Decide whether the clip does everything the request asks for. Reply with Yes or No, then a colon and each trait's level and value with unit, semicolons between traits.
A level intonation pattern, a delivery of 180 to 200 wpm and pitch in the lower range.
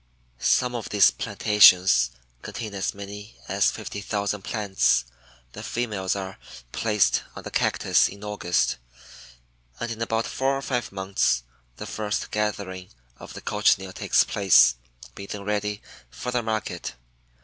No: narrow, 2.2 semitones; average, 140 wpm; low, 105 Hz